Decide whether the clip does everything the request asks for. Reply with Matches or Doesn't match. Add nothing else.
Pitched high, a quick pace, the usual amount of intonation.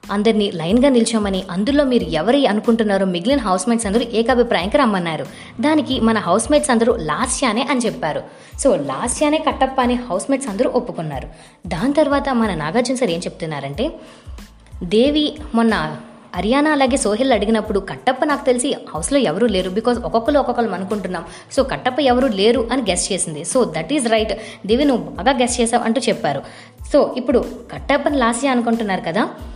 Matches